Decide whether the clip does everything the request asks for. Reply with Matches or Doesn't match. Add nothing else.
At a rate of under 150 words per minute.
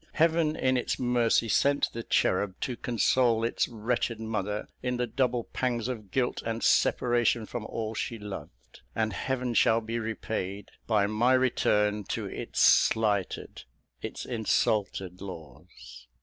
Matches